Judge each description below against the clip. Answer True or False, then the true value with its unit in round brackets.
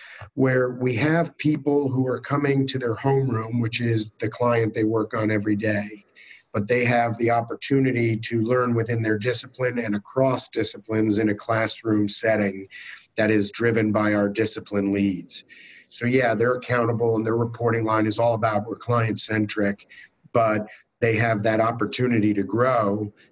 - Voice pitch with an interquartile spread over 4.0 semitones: False (2.4 semitones)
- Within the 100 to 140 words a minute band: False (165 wpm)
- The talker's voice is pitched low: True (115 Hz)